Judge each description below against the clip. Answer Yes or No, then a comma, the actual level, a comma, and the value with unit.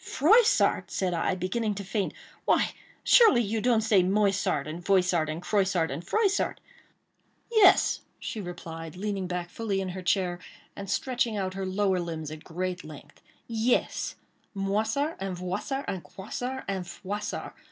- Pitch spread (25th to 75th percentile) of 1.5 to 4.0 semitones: Yes, average, 3.6 semitones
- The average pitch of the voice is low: No, high, 195 Hz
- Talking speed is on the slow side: No, average, 150 wpm